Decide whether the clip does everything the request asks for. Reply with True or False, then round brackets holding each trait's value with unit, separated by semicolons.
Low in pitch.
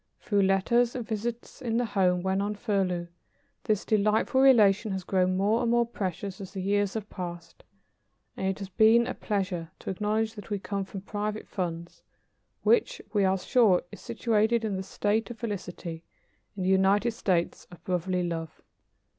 False (200 Hz)